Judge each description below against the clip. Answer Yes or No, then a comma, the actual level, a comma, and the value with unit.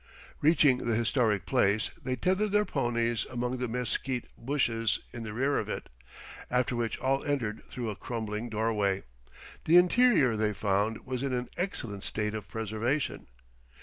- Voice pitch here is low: Yes, low, 120 Hz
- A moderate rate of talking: Yes, average, 155 wpm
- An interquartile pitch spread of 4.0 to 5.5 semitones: No, average, 3.5 semitones